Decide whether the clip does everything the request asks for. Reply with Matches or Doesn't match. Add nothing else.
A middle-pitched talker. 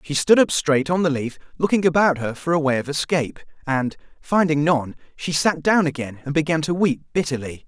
Matches